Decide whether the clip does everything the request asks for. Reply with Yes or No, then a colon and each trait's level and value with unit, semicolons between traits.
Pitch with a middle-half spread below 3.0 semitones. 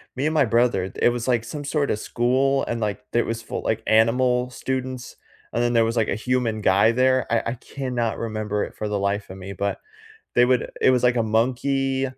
Yes: narrow, 2.6 semitones